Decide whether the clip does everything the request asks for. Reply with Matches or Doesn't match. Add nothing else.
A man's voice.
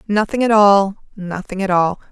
Doesn't match